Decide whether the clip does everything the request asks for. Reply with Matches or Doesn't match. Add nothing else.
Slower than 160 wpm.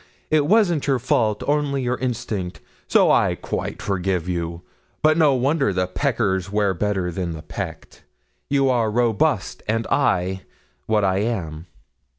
Matches